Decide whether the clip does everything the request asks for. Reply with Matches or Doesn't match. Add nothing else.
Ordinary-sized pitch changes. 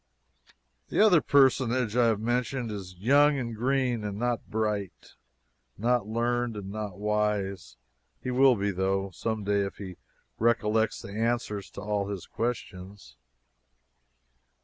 Matches